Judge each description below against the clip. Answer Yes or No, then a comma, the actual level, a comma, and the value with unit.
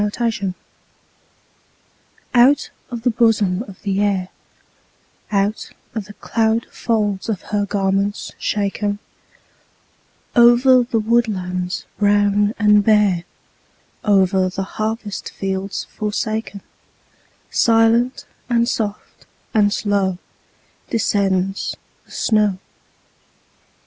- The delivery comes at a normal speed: No, slow, 95 wpm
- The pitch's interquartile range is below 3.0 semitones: Yes, narrow, 2.4 semitones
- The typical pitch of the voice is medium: No, high, 205 Hz